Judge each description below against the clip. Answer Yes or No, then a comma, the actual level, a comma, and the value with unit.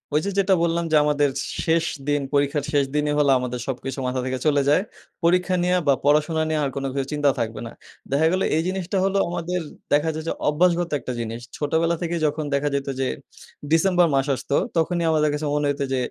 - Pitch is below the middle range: No, medium, 150 Hz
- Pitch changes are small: No, average, 3.3 semitones